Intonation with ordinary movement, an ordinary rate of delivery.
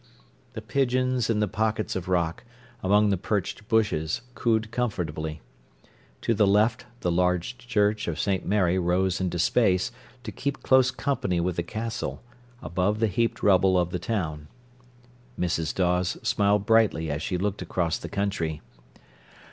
Yes: average, 3.9 semitones; average, 150 wpm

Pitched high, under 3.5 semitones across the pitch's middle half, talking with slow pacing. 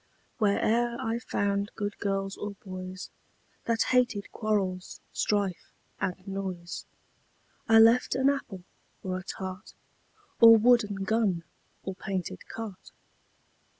Yes: high, 200 Hz; average, 3.1 semitones; slow, 115 wpm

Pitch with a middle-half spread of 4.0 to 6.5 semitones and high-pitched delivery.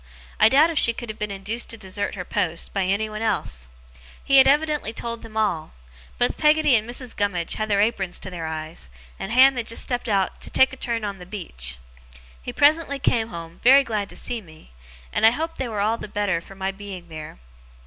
Yes: average, 4.6 semitones; high, 215 Hz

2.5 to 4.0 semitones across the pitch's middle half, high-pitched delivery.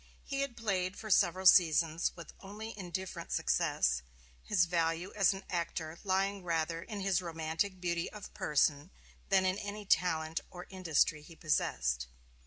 No: average, 3.1 semitones; medium, 180 Hz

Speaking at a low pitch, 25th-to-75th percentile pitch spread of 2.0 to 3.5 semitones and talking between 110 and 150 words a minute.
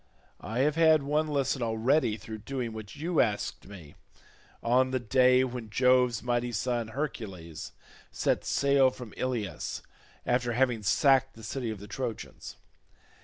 Yes: low, 125 Hz; average, 3.1 semitones; average, 145 wpm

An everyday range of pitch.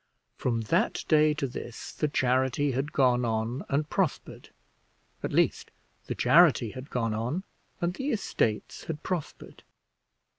Yes: average, 4.3 semitones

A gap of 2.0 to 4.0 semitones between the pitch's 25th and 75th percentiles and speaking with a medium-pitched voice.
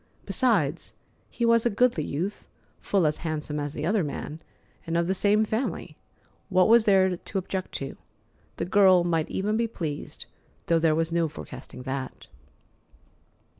No: average, 4.9 semitones; medium, 175 Hz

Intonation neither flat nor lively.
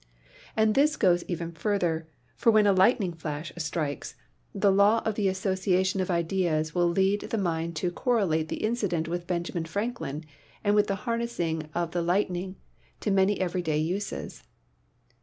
Yes: average, 3.5 semitones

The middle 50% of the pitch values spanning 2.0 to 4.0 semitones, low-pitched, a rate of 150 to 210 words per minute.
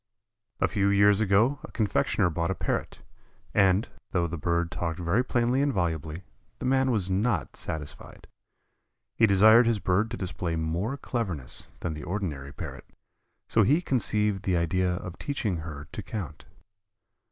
No: average, 4.6 semitones; very low, 95 Hz; average, 155 wpm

